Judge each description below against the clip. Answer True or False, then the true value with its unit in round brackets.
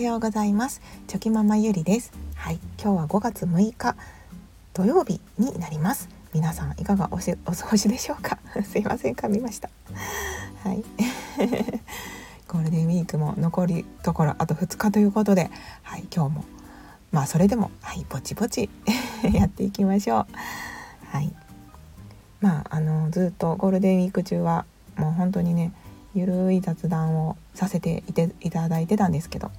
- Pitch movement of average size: True (4.2 semitones)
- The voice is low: False (185 Hz)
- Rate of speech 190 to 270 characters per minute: False (320 characters per minute)